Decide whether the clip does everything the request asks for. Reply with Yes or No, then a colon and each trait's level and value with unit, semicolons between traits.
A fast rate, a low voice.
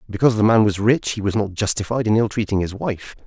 Yes: fast, 255 wpm; low, 105 Hz